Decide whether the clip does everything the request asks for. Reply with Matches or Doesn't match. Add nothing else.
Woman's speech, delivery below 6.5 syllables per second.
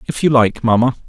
Doesn't match